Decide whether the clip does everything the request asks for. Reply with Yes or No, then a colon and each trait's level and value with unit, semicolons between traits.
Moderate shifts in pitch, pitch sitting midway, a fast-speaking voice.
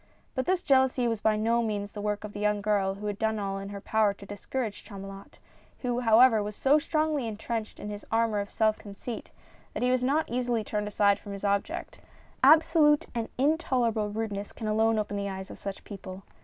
No: average, 3.2 semitones; high, 215 Hz; fast, 215 wpm